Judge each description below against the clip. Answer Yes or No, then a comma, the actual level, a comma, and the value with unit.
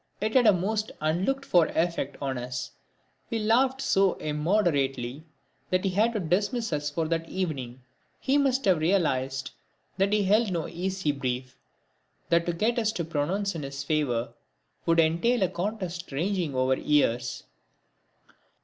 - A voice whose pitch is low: No, medium, 170 Hz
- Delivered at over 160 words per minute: No, average, 155 wpm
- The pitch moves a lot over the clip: Yes, wide, 6.1 semitones